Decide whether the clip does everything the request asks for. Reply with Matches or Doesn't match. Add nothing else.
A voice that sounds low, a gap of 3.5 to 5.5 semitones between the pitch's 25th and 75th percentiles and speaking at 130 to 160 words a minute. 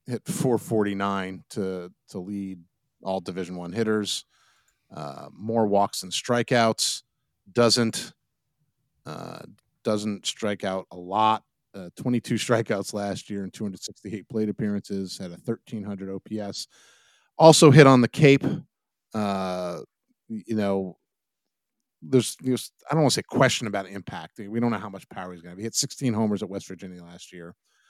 Matches